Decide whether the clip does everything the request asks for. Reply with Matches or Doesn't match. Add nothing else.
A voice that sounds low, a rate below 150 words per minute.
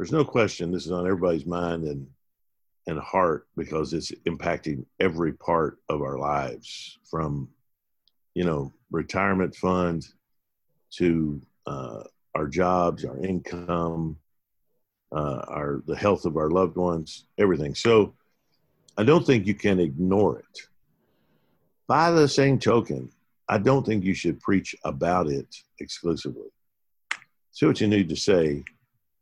Matches